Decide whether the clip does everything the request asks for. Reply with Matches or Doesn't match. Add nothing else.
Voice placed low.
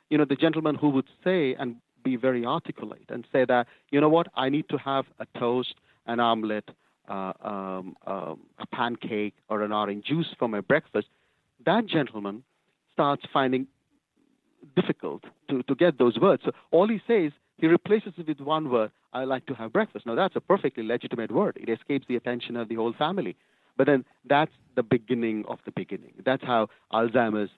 Matches